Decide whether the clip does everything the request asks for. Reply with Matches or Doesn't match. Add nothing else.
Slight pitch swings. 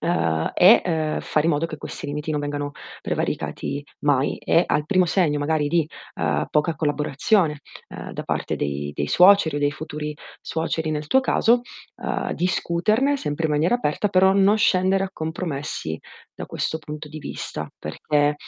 Doesn't match